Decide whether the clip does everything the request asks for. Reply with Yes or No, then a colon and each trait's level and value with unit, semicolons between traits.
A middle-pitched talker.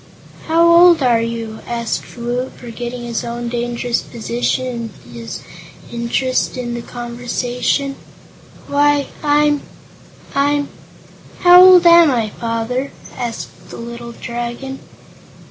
No: high, 245 Hz